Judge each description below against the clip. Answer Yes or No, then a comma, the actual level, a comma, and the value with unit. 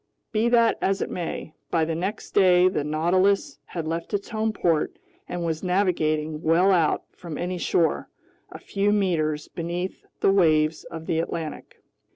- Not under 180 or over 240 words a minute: No, average, 165 wpm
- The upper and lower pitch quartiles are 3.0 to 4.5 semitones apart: Yes, average, 3.3 semitones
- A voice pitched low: No, medium, 175 Hz